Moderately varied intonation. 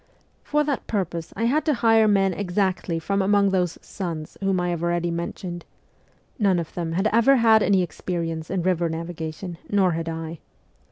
Yes: average, 3.3 semitones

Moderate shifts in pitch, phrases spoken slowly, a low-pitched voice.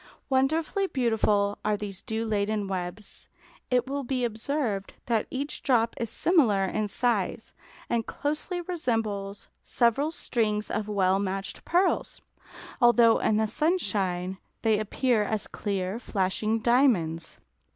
No: average, 4.0 semitones; slow, 125 wpm; high, 220 Hz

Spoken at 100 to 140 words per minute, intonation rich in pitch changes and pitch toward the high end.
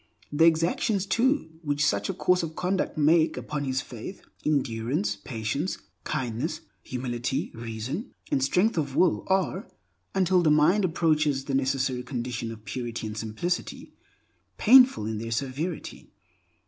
No: slow, 135 wpm; wide, 6.3 semitones; medium, 145 Hz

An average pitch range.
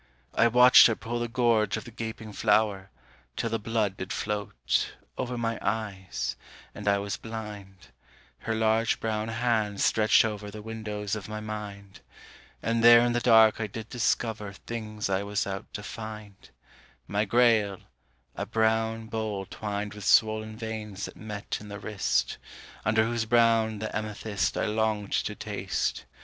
No: narrow, 1.5 semitones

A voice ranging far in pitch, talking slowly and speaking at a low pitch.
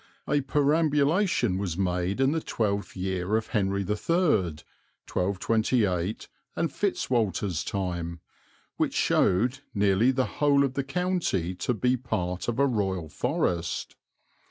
Yes: wide, 6.5 semitones; slow, 130 wpm; low, 105 Hz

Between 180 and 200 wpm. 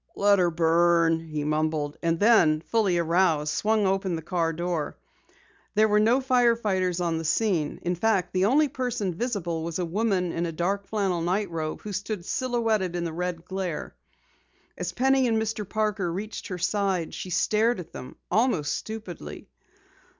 No: average, 170 wpm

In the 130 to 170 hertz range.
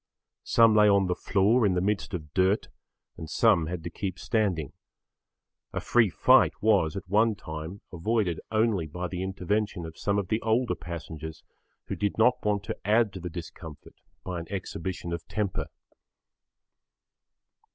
No: very low, 95 Hz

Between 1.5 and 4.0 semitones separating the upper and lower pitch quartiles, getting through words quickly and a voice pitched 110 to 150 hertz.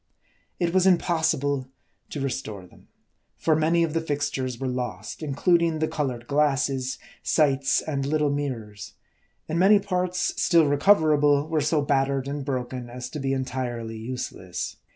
No: average, 3.6 semitones; average, 145 wpm; medium, 140 Hz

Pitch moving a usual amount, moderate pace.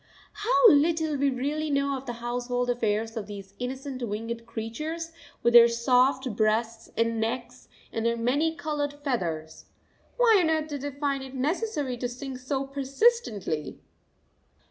Yes: average, 3.8 semitones; average, 150 wpm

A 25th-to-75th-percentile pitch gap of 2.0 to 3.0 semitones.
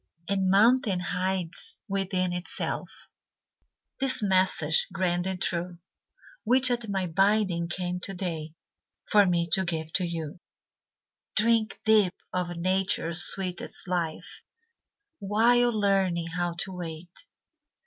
Yes: narrow, 2.5 semitones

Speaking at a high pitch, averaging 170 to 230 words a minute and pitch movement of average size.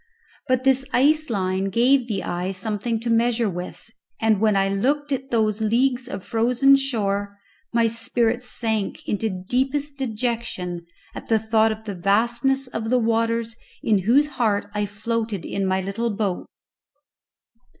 No: high, 225 Hz; average, 150 wpm; average, 3.5 semitones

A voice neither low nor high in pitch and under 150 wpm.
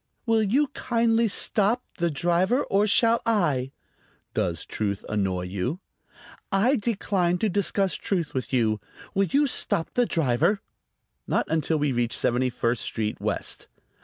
Yes: medium, 175 Hz; average, 140 wpm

